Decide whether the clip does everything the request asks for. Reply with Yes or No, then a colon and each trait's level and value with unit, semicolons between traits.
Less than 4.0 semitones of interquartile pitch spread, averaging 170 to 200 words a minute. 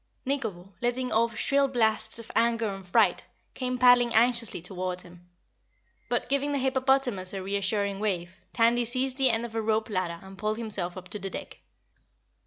No: average, 4.3 semitones; average, 175 wpm